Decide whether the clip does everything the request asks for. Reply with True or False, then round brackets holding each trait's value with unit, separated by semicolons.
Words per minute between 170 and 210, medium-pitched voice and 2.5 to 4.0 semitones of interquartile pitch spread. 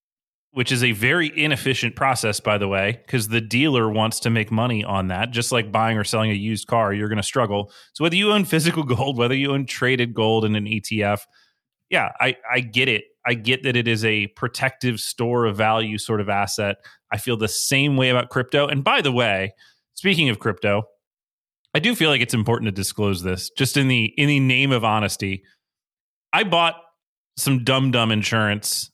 False (205 wpm; 115 Hz; 3.7 semitones)